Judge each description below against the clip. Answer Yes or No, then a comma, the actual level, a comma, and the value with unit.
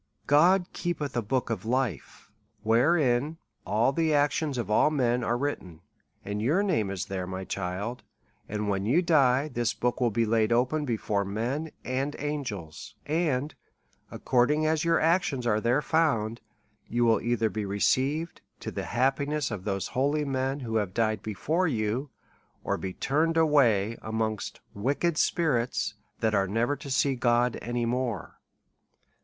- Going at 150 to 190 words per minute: Yes, average, 155 wpm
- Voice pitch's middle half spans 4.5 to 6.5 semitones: Yes, average, 5.2 semitones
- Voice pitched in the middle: No, low, 125 Hz